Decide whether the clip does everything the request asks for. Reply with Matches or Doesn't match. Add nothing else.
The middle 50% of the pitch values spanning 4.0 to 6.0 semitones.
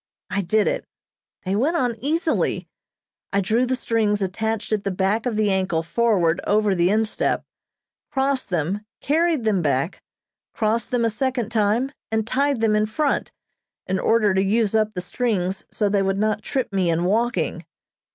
Doesn't match